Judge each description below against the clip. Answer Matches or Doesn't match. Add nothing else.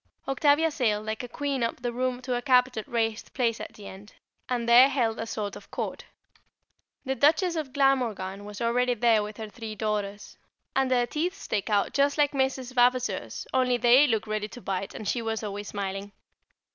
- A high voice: Matches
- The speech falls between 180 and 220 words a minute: Matches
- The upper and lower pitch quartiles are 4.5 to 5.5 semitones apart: Doesn't match